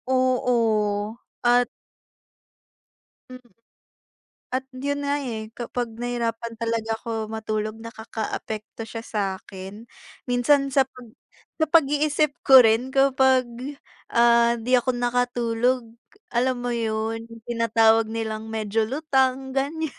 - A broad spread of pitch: No, narrow, 2.5 semitones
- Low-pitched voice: No, high, 235 Hz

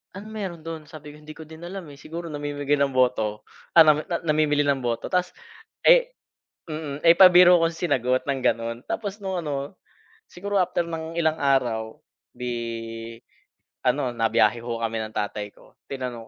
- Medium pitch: Yes, medium, 145 Hz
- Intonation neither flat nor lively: No, wide, 5.7 semitones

